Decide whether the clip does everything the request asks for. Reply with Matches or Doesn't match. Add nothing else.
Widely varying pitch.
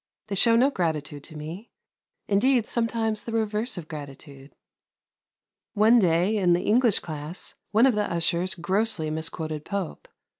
Matches